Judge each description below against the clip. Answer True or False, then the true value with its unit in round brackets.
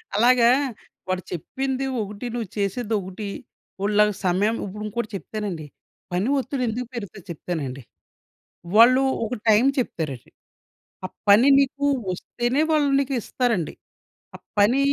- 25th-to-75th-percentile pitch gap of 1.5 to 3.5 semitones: False (4.7 semitones)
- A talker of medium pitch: False (215 Hz)